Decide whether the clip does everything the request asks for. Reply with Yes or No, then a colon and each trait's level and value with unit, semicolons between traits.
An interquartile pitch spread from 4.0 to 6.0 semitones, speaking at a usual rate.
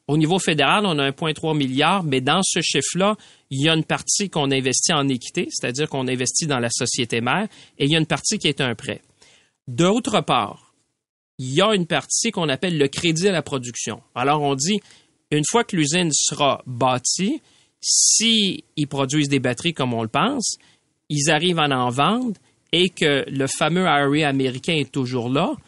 Yes: average, 4.7 semitones; average, 195 wpm